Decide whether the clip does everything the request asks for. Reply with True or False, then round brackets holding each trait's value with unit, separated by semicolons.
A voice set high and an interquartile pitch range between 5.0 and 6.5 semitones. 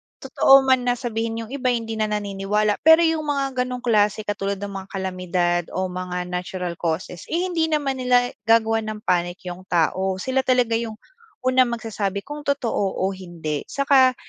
True (220 Hz; 5.3 semitones)